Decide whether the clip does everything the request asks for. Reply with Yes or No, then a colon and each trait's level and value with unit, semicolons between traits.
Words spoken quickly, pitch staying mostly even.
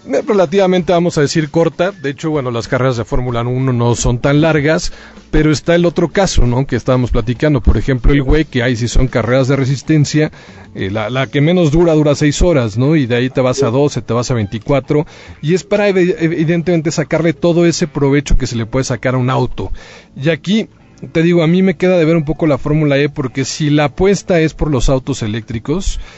No: fast, 225 wpm; average, 4.6 semitones